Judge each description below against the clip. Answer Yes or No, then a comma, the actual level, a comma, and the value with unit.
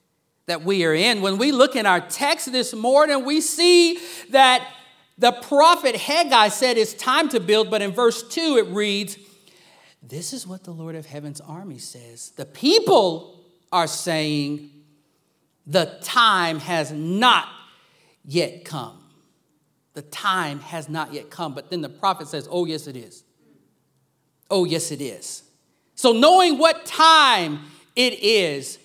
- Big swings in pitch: Yes, wide, 8.2 semitones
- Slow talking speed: No, average, 150 wpm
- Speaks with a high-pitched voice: Yes, high, 195 Hz